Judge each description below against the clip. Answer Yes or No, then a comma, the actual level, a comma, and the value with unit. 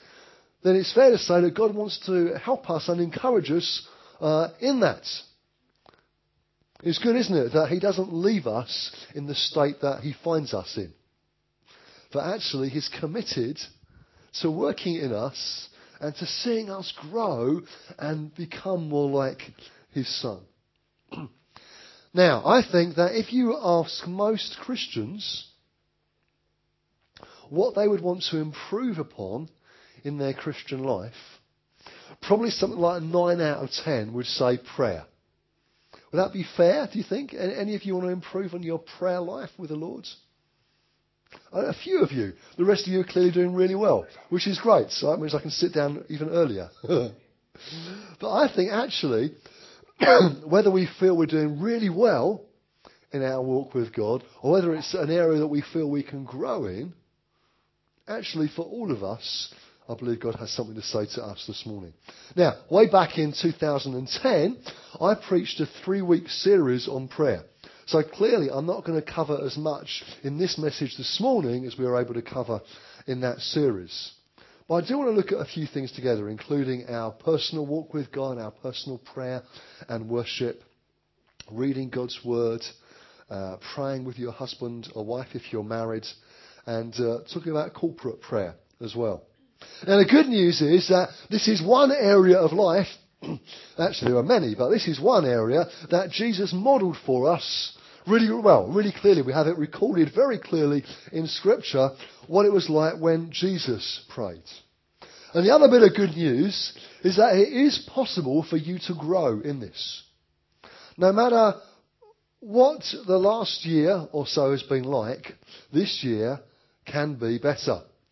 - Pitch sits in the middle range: Yes, medium, 165 Hz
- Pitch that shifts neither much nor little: No, wide, 6.2 semitones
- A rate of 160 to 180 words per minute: Yes, average, 170 wpm